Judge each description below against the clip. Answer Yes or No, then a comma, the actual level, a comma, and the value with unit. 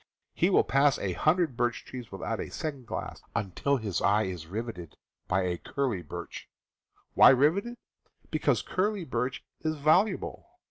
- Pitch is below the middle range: Yes, low, 125 Hz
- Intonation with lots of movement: Yes, wide, 7.8 semitones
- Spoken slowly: No, average, 150 wpm